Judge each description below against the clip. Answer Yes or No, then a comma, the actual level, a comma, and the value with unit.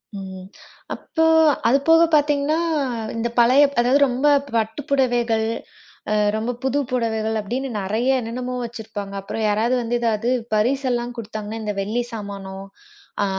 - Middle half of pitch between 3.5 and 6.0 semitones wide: No, average, 3.0 semitones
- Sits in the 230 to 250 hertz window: Yes, high, 235 Hz